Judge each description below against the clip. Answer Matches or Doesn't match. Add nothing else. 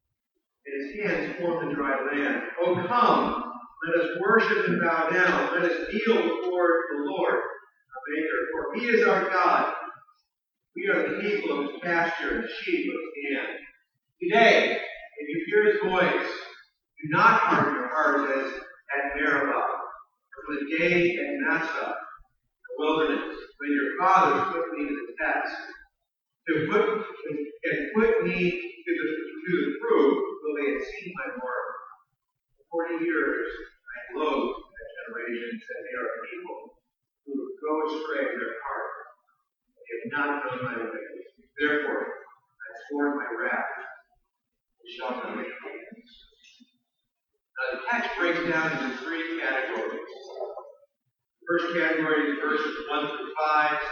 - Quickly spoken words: Doesn't match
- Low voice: Doesn't match